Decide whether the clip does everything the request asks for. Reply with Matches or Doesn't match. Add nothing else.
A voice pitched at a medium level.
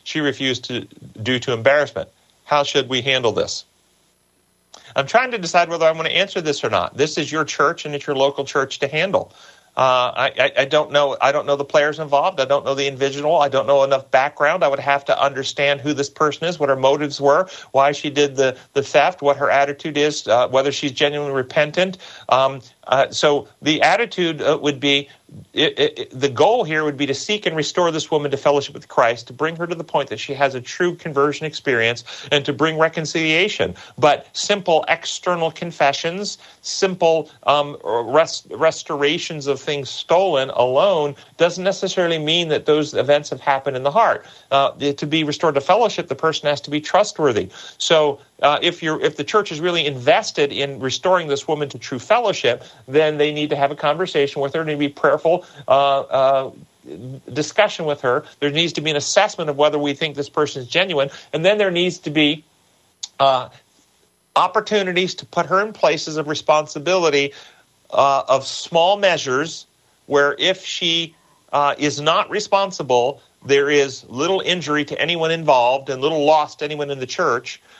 Matches